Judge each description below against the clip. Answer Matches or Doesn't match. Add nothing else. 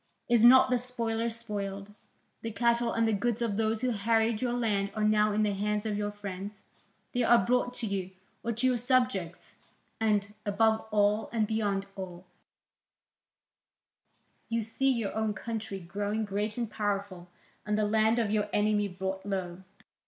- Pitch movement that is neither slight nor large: Doesn't match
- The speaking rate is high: Doesn't match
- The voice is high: Matches